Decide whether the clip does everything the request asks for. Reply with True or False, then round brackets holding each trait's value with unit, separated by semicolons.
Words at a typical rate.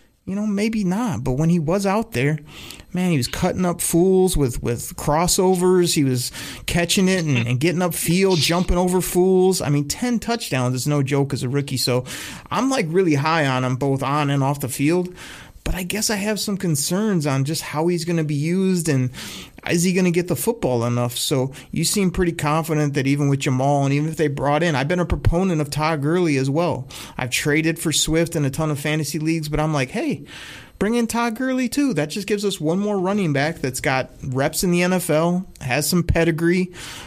False (220 wpm)